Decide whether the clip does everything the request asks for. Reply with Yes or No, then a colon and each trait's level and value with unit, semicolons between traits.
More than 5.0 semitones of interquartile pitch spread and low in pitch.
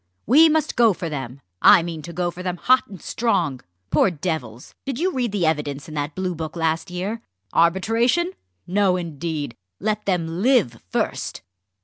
No: wide, 5.6 semitones; medium, 180 Hz